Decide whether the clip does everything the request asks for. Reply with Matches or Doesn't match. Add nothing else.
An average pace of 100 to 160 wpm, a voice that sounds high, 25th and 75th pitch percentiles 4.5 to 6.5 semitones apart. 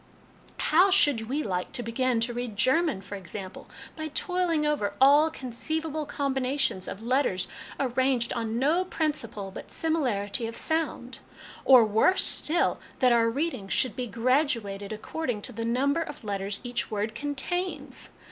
Matches